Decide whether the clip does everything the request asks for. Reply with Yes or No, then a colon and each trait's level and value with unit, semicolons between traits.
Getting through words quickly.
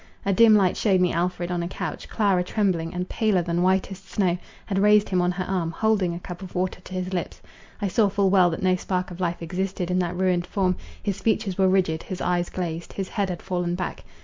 Yes: fast, 235 wpm